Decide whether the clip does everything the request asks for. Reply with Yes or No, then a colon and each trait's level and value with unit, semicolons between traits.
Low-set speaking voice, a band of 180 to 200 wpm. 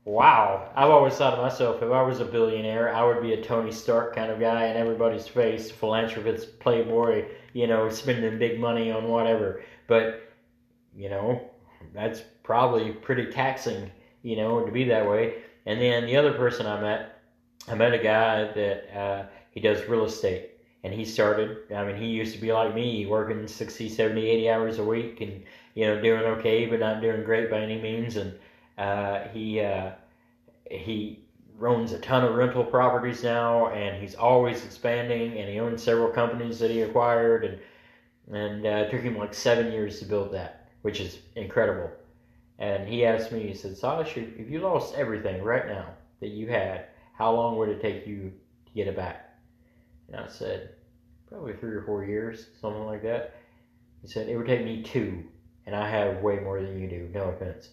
Yes: low, 115 Hz; average, 190 wpm